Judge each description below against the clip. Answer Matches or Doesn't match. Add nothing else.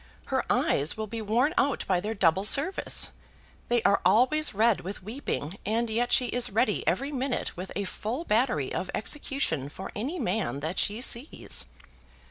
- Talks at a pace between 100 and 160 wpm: Doesn't match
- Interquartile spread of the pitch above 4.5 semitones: Matches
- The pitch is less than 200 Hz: Doesn't match